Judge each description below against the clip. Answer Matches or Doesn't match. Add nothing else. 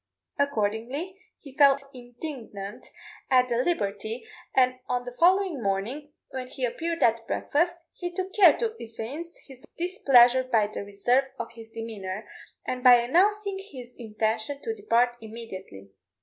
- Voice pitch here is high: Matches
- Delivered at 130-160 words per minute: Matches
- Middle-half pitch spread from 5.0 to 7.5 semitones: Matches